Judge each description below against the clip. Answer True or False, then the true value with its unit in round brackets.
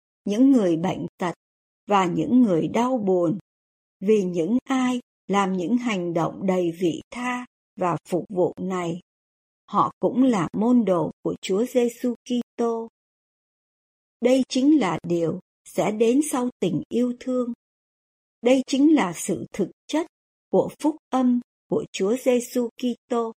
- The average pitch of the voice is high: True (230 Hz)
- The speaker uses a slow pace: True (140 wpm)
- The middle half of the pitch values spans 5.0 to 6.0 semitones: True (5.6 semitones)